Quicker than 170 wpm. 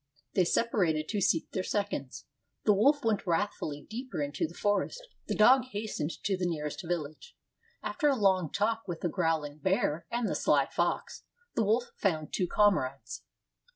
No: average, 165 wpm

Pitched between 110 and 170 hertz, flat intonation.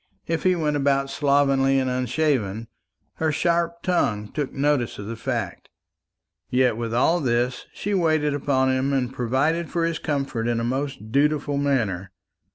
No: low, 135 Hz; average, 3.7 semitones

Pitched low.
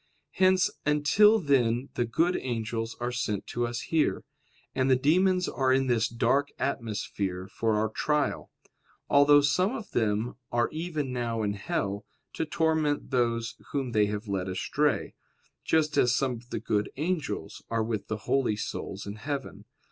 Yes: low, 125 Hz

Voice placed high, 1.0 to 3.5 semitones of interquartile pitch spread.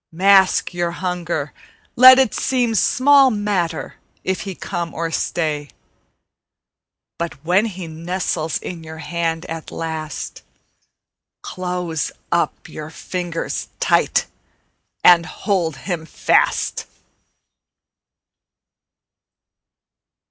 No: medium, 175 Hz; average, 2.8 semitones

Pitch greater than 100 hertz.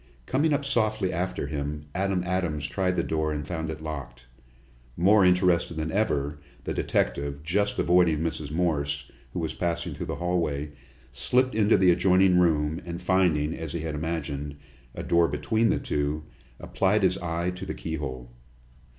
No: very low, 85 Hz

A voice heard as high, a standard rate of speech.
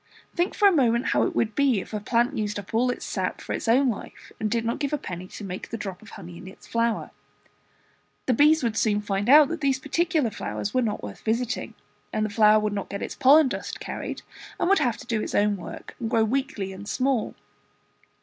No: high, 230 Hz; fast, 235 wpm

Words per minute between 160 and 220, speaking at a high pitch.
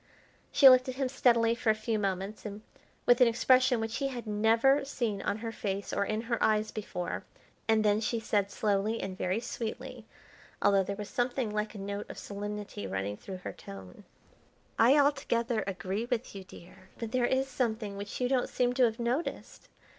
Yes: average, 190 wpm; high, 220 Hz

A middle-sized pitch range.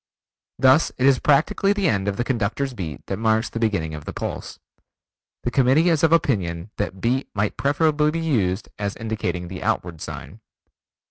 No: wide, 6.4 semitones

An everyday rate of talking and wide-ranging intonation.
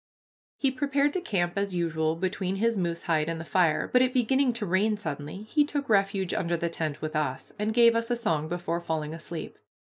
No: fast, 210 wpm; wide, 6.0 semitones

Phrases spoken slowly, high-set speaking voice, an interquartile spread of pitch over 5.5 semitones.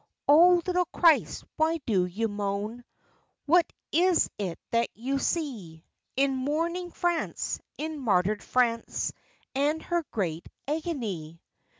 Yes: slow, 115 wpm; very high, 270 Hz; wide, 8.1 semitones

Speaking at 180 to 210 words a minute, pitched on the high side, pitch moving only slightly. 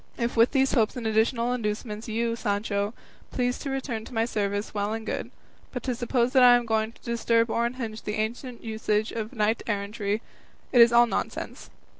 Yes: average, 190 wpm; high, 230 Hz; narrow, 1.9 semitones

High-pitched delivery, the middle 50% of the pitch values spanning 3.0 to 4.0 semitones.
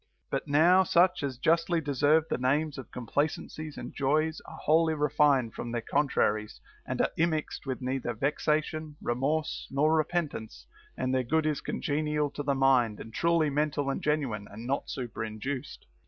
No: medium, 145 Hz; average, 3.3 semitones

